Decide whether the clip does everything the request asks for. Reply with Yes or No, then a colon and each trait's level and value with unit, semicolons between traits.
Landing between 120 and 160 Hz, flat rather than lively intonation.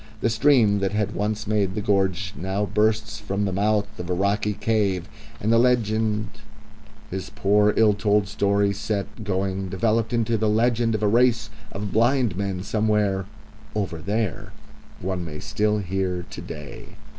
No: low, 105 Hz; narrow, 2.0 semitones